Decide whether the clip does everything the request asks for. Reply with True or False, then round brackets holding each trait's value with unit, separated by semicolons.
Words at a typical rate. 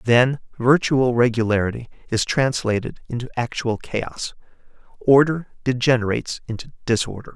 False (100 wpm)